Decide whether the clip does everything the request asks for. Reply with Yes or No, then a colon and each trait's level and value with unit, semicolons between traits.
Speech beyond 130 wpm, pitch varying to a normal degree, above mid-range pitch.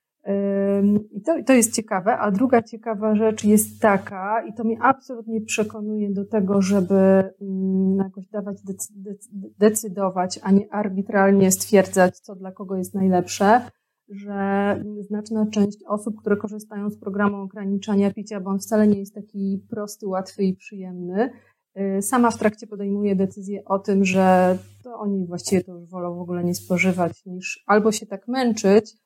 No: average, 155 wpm; narrow, 1.7 semitones; high, 200 Hz